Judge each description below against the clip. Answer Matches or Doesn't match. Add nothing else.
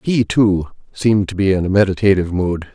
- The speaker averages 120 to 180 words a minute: Doesn't match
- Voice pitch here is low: Matches